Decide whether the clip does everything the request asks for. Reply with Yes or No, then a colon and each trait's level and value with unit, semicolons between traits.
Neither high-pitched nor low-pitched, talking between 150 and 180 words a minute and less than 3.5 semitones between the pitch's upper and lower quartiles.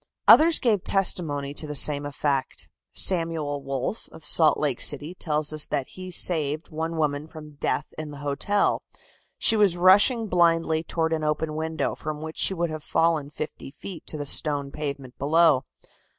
Yes: medium, 155 Hz; average, 170 wpm; narrow, 2.6 semitones